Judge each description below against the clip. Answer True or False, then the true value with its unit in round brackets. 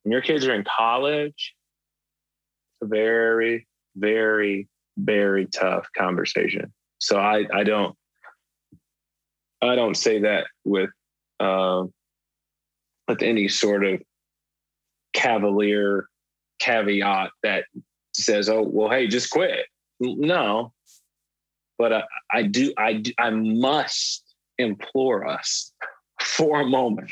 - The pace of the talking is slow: True (110 wpm)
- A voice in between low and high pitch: False (110 Hz)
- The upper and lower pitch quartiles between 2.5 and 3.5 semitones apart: True (2.8 semitones)